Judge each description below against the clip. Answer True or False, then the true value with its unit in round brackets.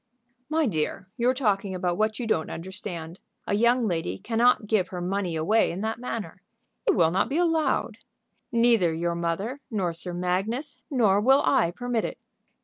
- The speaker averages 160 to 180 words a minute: True (170 wpm)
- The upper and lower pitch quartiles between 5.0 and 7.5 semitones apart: True (5.3 semitones)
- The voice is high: True (205 Hz)